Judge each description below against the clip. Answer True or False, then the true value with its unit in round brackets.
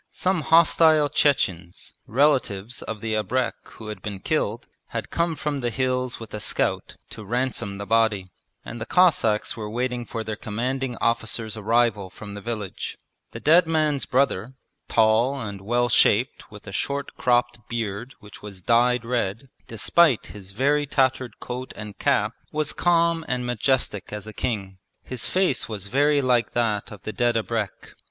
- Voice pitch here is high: False (120 Hz)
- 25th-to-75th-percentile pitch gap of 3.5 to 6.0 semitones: True (4.0 semitones)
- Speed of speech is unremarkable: True (165 wpm)